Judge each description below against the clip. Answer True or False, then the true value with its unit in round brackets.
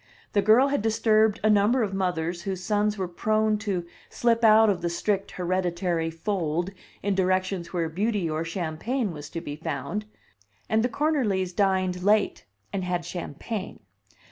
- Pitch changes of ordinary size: True (3.8 semitones)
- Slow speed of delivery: False (160 wpm)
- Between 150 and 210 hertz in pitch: True (190 Hz)